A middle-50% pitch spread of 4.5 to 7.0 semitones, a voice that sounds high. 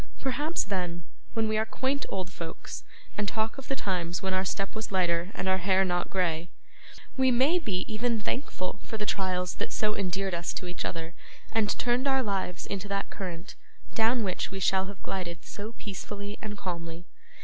No: average, 3.5 semitones; high, 195 Hz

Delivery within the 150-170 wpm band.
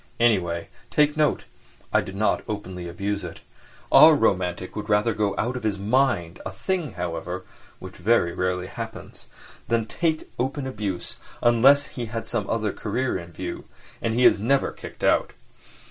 Yes: average, 160 wpm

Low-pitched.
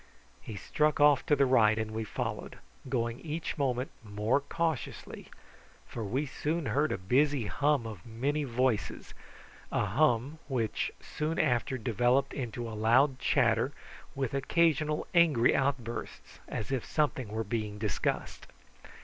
Yes: low, 130 Hz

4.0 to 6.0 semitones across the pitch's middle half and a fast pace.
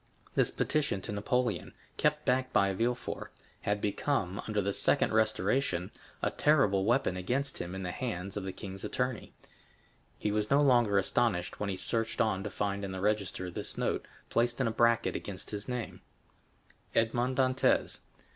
No: average, 4.3 semitones; average, 165 wpm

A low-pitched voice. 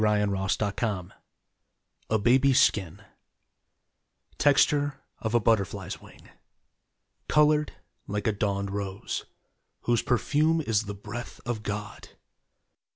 Yes: low, 110 Hz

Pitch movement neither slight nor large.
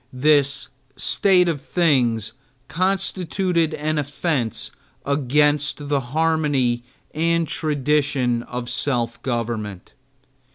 Yes: average, 4.5 semitones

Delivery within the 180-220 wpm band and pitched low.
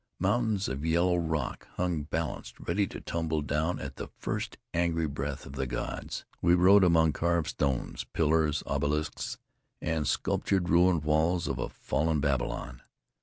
No: average, 150 wpm; very low, 80 Hz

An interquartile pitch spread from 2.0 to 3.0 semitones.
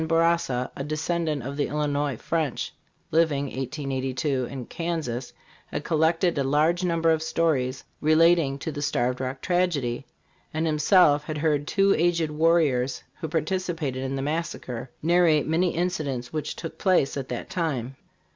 No: average, 3.6 semitones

